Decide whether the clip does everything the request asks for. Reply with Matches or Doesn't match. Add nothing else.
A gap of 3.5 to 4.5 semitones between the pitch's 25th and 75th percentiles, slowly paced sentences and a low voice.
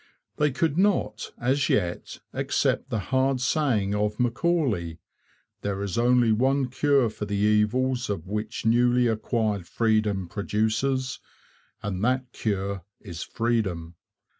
Matches